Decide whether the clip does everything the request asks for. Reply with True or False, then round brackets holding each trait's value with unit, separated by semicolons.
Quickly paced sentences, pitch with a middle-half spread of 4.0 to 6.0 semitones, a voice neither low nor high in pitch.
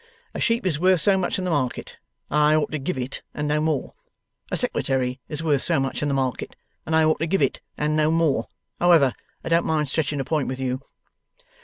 False (230 wpm; 3.3 semitones; 150 Hz)